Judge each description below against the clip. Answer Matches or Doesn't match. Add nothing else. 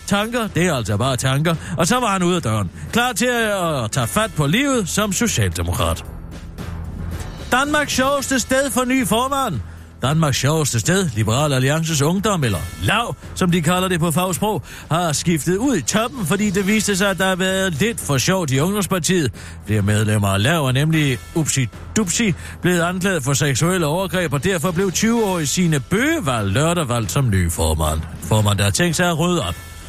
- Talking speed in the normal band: Matches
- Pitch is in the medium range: Matches